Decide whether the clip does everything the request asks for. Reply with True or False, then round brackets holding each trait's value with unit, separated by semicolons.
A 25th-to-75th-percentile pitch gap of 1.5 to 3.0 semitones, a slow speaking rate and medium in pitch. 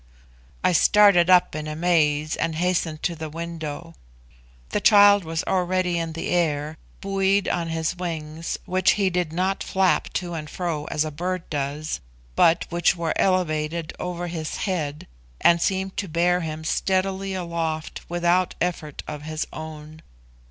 False (2.6 semitones; 150 wpm; 170 Hz)